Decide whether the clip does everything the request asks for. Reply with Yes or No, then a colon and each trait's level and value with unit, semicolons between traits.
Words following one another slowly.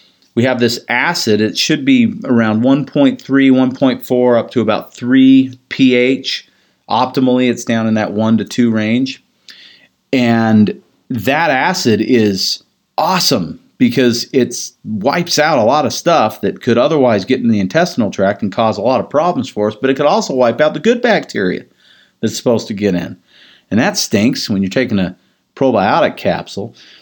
No: average, 170 wpm